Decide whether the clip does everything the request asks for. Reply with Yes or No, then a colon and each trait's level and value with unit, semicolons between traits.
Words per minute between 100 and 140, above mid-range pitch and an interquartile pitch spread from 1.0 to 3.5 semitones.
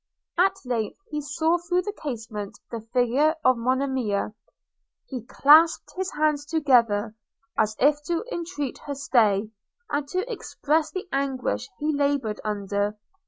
No: slow, 135 wpm; very high, 275 Hz; wide, 5.6 semitones